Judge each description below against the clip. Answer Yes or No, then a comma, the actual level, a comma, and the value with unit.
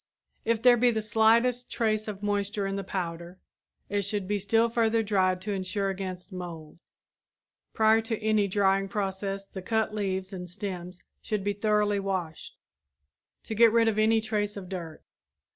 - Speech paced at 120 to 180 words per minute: Yes, average, 165 wpm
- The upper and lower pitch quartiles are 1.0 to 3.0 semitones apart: Yes, narrow, 2.5 semitones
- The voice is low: No, high, 205 Hz